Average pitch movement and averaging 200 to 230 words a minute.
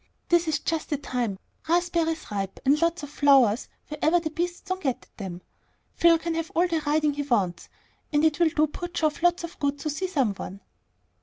Yes: average, 3.7 semitones; fast, 205 wpm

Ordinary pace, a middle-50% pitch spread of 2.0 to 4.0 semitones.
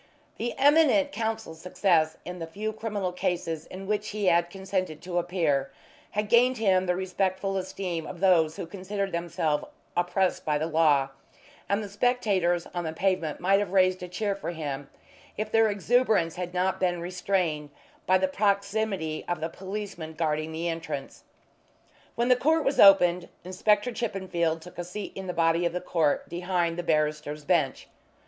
Yes: average, 170 wpm; average, 3.2 semitones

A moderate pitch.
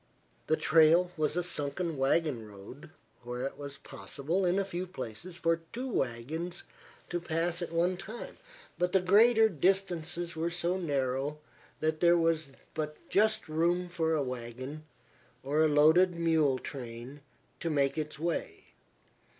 Yes: medium, 160 Hz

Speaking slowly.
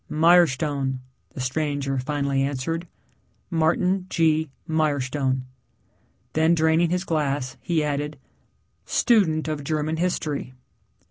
Yes: slow, 95 wpm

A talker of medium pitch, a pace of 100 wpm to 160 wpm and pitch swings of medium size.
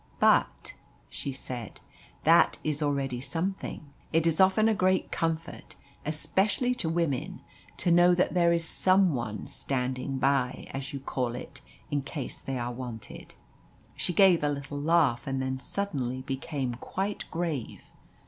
Yes: medium, 145 Hz; average, 150 wpm; average, 4.7 semitones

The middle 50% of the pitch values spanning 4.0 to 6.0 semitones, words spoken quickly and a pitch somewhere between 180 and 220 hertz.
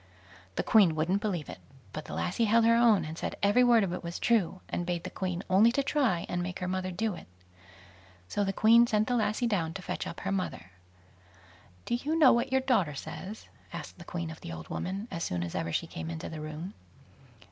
Yes: average, 5.2 semitones; fast, 230 wpm; high, 190 Hz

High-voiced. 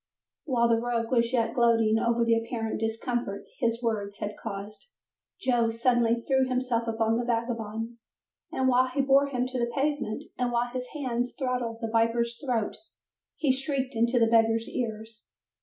Yes: high, 235 Hz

